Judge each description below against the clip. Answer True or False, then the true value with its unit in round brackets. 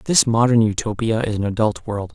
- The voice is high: False (110 Hz)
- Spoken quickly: False (195 wpm)